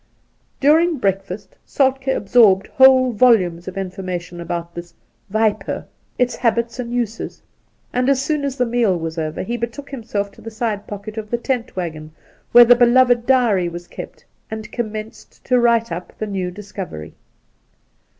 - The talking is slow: No, average, 175 wpm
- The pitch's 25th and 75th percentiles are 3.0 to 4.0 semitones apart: No, average, 4.7 semitones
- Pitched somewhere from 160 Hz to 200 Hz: No, high, 220 Hz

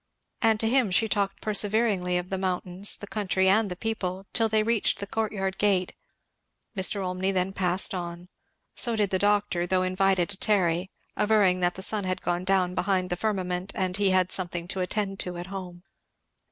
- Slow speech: No, average, 190 wpm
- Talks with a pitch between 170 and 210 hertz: Yes, high, 190 Hz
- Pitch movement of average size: No, narrow, 2.1 semitones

